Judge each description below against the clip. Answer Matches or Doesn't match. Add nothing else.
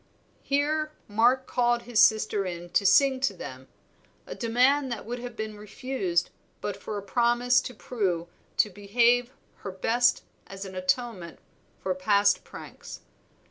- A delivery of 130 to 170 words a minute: Matches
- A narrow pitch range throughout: Doesn't match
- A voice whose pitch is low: Doesn't match